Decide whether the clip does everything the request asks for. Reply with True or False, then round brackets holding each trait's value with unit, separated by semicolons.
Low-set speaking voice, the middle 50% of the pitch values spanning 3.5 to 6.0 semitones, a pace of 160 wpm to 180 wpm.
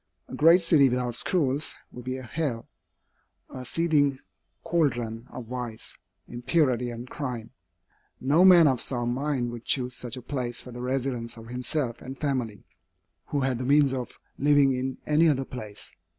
False (130 Hz; 3.0 semitones; 165 wpm)